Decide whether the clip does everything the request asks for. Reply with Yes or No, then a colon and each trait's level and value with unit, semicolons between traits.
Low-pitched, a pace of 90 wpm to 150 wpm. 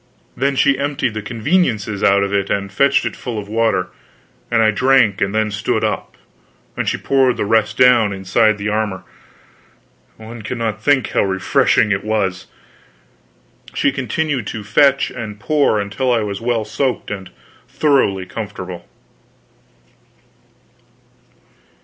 Yes: low, 110 Hz; average, 140 wpm